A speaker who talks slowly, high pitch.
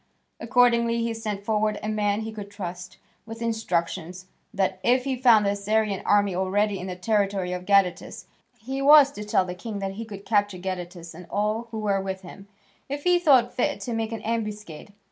No: average, 195 wpm; high, 210 Hz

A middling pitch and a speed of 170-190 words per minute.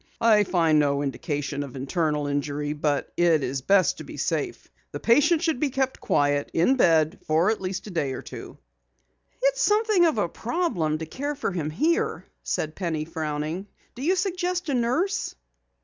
Yes: medium, 175 Hz; average, 180 wpm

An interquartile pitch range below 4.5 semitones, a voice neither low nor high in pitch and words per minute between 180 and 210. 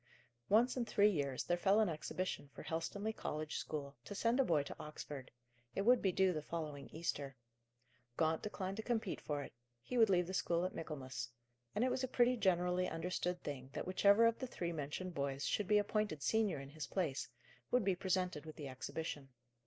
No: wide, 5.6 semitones; medium, 180 Hz; average, 200 wpm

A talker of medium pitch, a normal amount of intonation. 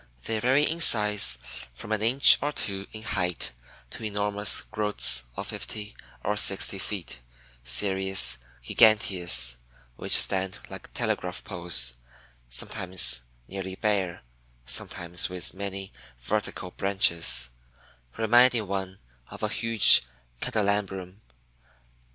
No: very low, 95 Hz; average, 3.0 semitones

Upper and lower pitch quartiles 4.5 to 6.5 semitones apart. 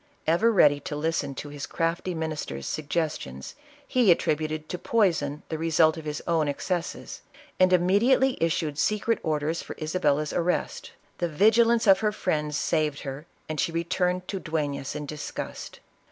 No: average, 3.4 semitones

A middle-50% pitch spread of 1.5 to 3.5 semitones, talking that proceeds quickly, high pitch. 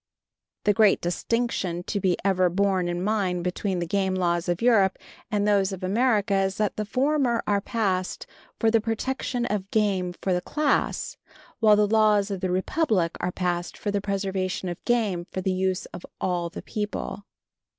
No: average, 2.7 semitones; average, 180 wpm; high, 195 Hz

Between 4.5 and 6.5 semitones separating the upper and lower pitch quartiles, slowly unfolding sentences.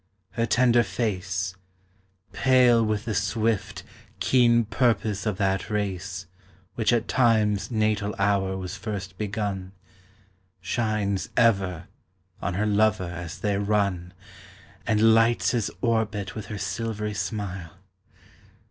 No: average, 2.8 semitones; slow, 115 wpm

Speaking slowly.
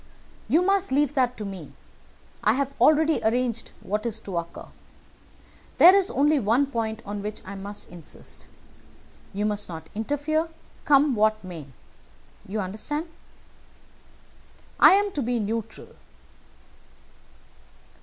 Yes: slow, 125 wpm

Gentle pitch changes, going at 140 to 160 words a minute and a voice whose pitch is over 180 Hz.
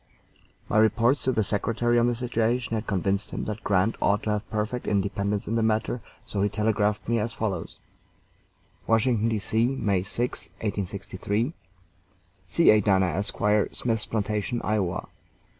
No: narrow, 2.3 semitones; average, 150 wpm; low, 110 Hz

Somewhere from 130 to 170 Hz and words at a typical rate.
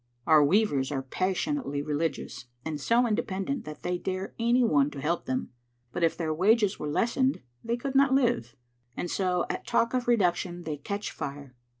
No: medium, 180 Hz; average, 180 wpm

